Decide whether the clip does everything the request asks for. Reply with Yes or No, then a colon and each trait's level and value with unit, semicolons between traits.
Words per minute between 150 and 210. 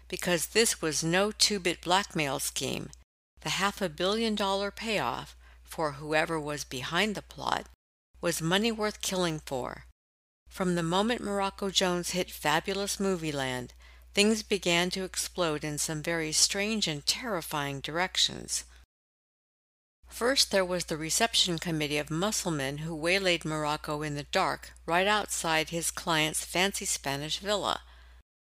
No: slow, 135 wpm